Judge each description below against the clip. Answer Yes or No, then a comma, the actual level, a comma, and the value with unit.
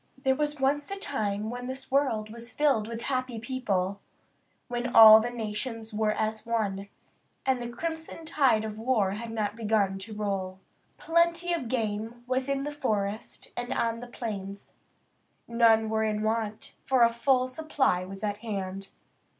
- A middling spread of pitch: Yes, average, 3.6 semitones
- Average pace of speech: Yes, average, 165 wpm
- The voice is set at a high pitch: Yes, high, 230 Hz